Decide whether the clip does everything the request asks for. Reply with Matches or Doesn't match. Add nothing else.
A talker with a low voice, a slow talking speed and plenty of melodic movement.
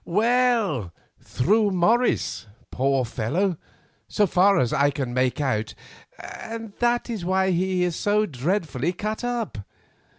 Doesn't match